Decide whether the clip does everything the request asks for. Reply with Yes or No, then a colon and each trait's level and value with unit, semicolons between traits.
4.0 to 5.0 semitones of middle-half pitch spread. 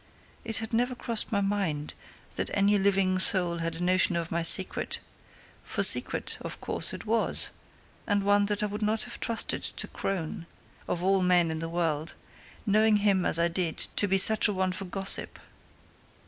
No: average, 3.2 semitones